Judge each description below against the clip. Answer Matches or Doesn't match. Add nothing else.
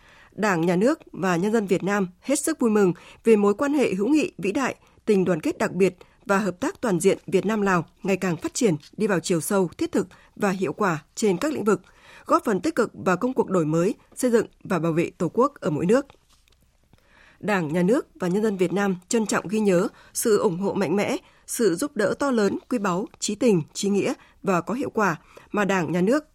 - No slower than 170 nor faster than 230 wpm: Doesn't match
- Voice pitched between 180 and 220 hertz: Matches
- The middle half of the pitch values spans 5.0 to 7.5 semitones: Doesn't match